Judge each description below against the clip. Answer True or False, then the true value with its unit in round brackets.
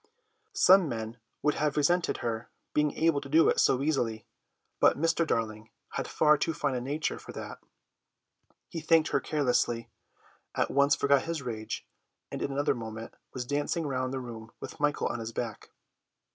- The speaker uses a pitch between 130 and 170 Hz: True (140 Hz)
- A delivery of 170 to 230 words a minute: True (175 wpm)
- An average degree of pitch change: True (4.5 semitones)